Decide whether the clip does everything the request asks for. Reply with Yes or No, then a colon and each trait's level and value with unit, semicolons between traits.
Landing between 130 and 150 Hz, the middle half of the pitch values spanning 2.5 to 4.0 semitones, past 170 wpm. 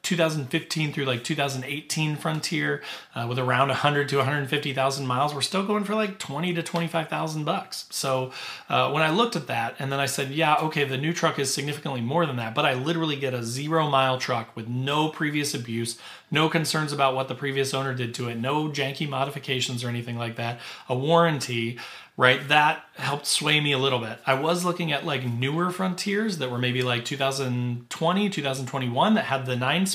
Yes: medium, 140 Hz; average, 3.6 semitones; average, 200 wpm